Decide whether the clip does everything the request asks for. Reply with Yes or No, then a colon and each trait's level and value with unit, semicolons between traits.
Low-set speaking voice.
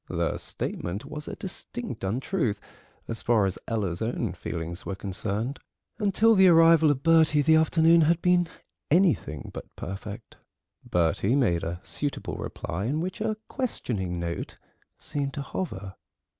Yes: low, 130 Hz